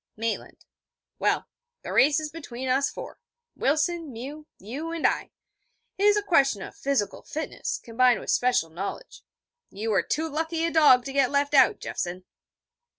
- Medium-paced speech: Yes, average, 160 wpm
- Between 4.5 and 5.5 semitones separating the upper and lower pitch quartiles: Yes, average, 4.8 semitones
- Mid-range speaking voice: No, very high, 280 Hz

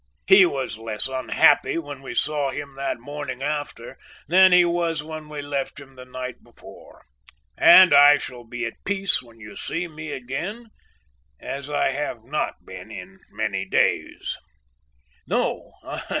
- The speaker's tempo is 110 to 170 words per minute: Yes, average, 150 wpm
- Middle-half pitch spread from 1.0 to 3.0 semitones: No, average, 3.5 semitones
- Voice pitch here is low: No, medium, 145 Hz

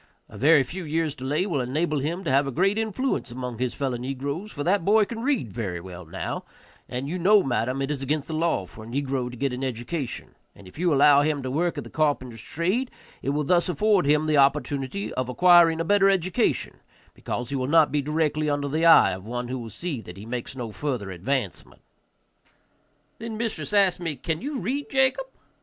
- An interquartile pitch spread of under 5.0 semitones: No, wide, 5.5 semitones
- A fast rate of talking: Yes, fast, 215 wpm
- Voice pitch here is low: No, medium, 145 Hz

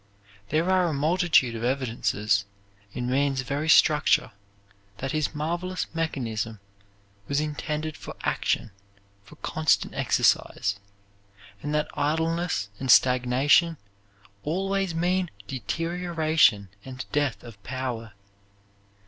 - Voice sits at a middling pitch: Yes, medium, 145 Hz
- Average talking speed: No, slow, 105 wpm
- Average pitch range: Yes, average, 4.6 semitones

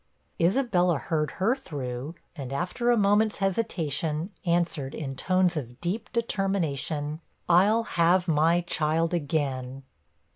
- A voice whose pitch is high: No, medium, 170 Hz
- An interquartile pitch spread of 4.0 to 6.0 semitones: Yes, average, 4.7 semitones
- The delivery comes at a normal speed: No, slow, 115 wpm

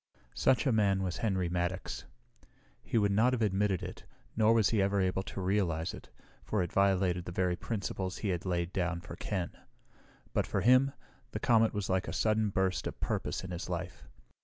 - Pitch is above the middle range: No, very low, 95 Hz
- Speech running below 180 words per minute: No, average, 195 wpm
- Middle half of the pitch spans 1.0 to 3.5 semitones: Yes, average, 2.9 semitones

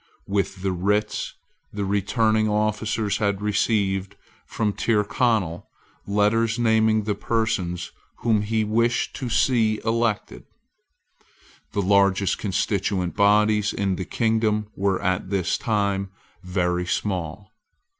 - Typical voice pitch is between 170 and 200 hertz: No, low, 105 Hz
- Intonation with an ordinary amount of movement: No, narrow, 2.0 semitones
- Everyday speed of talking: No, slow, 110 wpm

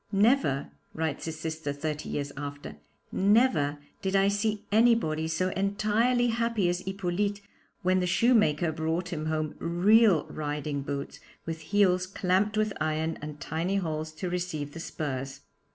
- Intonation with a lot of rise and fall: No, average, 4.7 semitones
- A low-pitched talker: No, medium, 175 Hz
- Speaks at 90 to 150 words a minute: Yes, average, 145 wpm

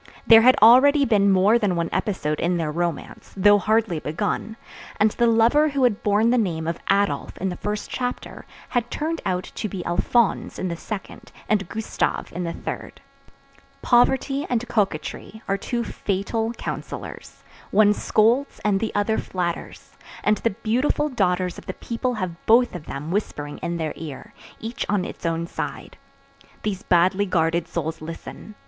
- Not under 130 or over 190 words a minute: Yes, average, 165 wpm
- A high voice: Yes, high, 205 Hz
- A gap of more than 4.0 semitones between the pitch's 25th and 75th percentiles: Yes, average, 4.7 semitones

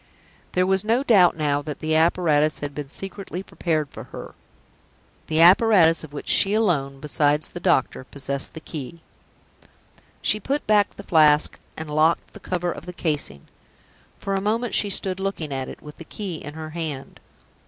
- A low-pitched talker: No, medium, 160 Hz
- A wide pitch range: No, average, 4.4 semitones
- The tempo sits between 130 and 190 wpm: Yes, average, 175 wpm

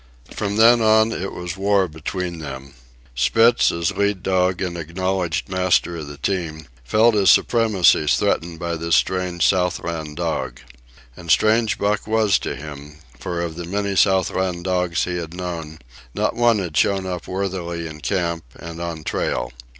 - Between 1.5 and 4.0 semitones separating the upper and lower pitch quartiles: Yes, average, 2.9 semitones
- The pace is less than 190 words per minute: Yes, average, 160 wpm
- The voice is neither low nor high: No, very low, 90 Hz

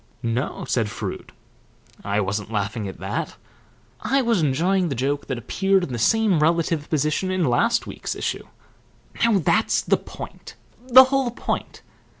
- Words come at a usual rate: Yes, average, 150 wpm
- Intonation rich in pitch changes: Yes, wide, 8.6 semitones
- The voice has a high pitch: No, medium, 155 Hz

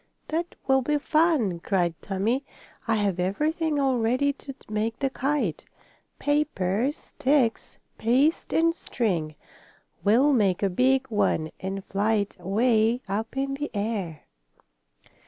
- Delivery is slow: Yes, slow, 130 wpm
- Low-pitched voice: No, high, 230 Hz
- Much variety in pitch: Yes, wide, 6.0 semitones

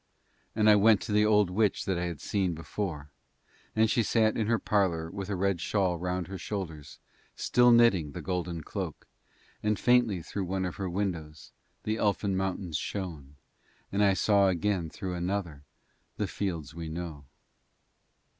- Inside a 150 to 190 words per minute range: Yes, average, 165 wpm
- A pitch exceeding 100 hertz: No, very low, 95 Hz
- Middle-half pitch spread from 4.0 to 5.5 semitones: No, average, 3.6 semitones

